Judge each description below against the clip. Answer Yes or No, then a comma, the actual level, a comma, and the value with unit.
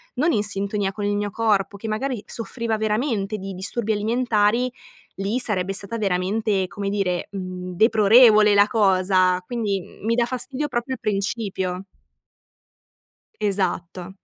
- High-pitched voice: Yes, high, 205 Hz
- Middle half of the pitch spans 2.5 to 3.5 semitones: Yes, average, 2.8 semitones